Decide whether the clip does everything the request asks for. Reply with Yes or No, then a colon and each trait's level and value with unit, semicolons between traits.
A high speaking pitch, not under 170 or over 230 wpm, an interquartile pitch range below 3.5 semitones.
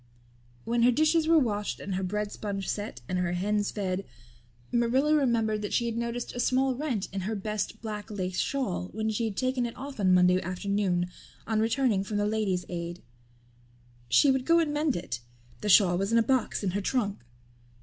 No: high, 215 Hz; average, 200 wpm; average, 4.2 semitones